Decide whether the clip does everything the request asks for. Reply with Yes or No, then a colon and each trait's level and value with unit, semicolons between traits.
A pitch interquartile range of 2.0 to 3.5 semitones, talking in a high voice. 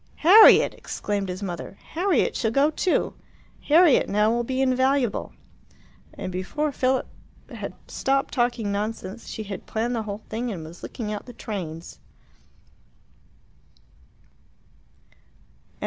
No: average, 4.8 semitones; high, 230 Hz